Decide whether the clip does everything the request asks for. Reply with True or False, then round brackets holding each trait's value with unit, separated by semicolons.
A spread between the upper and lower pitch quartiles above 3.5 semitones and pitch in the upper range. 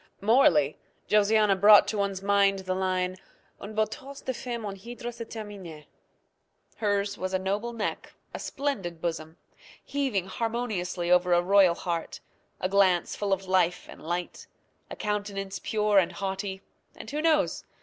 False (2.8 semitones; 200 Hz)